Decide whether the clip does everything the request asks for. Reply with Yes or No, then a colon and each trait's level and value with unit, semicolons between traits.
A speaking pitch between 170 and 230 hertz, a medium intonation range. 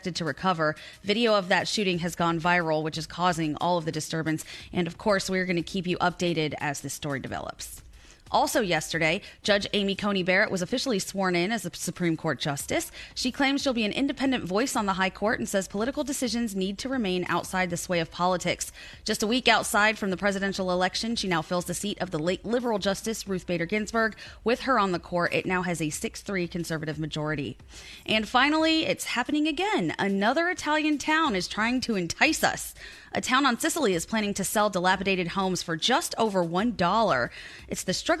Yes: high, 190 Hz; average, 4.6 semitones